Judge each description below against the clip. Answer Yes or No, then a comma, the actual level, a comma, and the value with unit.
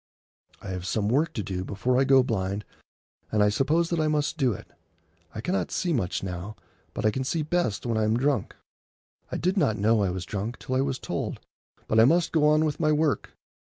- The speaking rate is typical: No, fast, 225 wpm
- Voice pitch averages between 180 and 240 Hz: No, low, 125 Hz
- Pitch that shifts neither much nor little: No, wide, 6.7 semitones